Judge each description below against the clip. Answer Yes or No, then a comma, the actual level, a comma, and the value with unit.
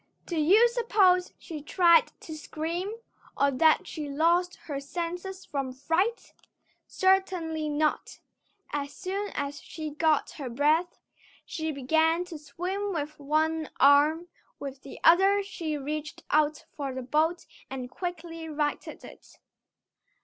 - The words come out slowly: Yes, slow, 130 wpm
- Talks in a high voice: Yes, very high, 315 Hz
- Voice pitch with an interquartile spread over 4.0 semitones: No, average, 3.4 semitones